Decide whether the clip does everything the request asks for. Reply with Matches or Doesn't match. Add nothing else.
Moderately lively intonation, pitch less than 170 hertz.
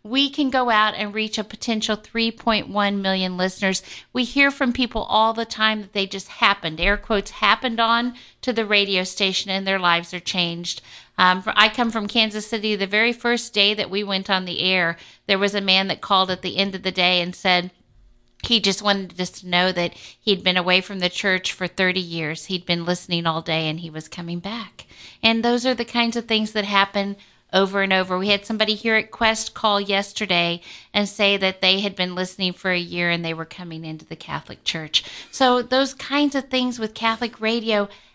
Doesn't match